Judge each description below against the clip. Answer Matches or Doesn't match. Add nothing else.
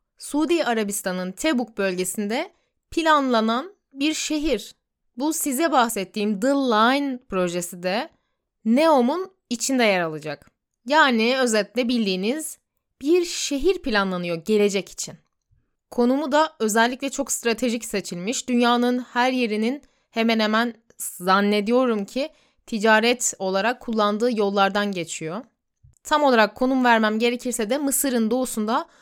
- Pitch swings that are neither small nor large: Matches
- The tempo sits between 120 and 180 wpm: Doesn't match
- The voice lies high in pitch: Matches